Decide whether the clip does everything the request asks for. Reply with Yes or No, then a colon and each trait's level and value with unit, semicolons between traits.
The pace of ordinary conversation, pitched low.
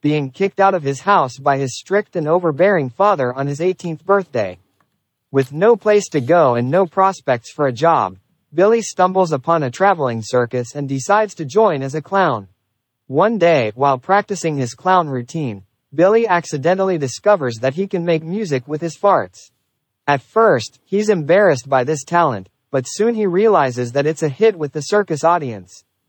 No: average, 175 wpm; medium, 155 Hz